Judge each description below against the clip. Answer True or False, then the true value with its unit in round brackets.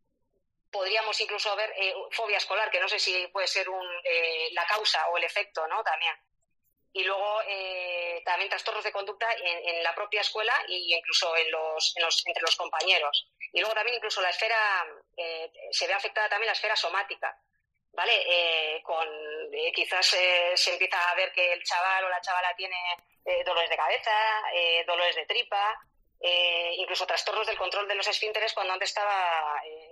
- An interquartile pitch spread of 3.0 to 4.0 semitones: True (3.4 semitones)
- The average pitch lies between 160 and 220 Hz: True (185 Hz)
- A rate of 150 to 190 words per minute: True (185 wpm)